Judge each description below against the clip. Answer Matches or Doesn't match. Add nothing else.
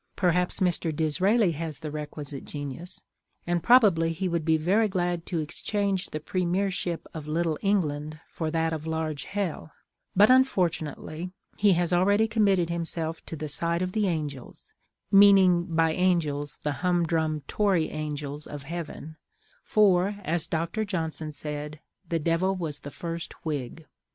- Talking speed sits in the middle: Matches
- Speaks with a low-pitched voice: Doesn't match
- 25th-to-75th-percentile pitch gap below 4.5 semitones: Matches